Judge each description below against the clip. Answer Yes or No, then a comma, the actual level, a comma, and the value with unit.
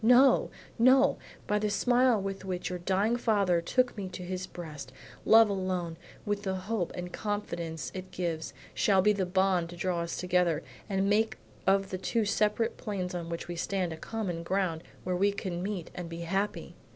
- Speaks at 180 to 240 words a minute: Yes, average, 190 wpm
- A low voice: No, high, 190 Hz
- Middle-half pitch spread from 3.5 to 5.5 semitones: No, average, 2.9 semitones